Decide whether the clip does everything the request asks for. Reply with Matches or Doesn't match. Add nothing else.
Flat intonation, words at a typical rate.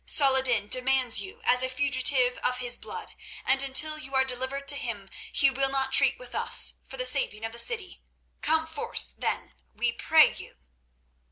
Matches